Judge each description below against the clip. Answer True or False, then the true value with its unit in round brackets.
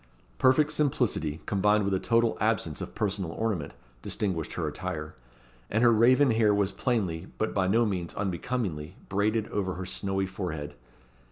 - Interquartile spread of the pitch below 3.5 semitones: False (4.0 semitones)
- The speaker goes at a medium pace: True (155 wpm)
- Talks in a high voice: False (100 Hz)